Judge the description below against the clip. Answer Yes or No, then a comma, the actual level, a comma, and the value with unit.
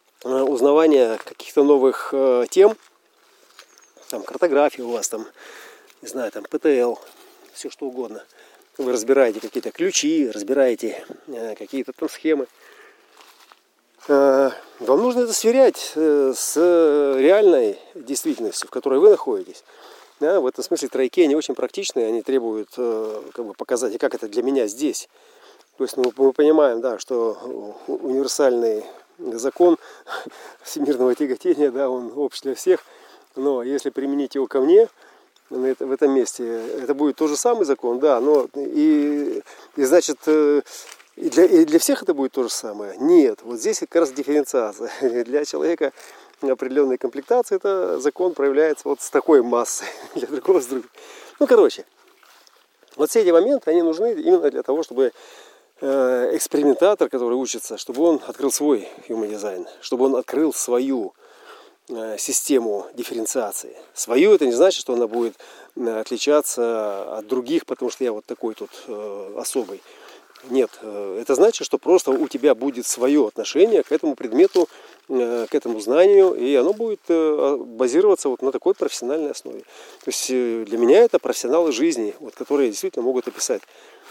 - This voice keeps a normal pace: Yes, average, 145 wpm